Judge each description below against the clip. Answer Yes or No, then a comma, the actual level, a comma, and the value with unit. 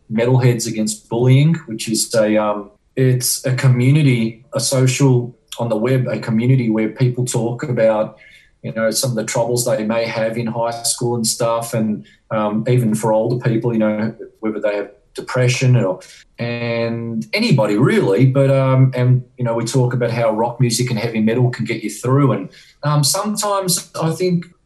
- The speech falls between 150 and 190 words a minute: Yes, average, 180 wpm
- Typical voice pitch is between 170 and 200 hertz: No, low, 120 Hz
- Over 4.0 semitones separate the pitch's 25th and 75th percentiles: No, narrow, 2.6 semitones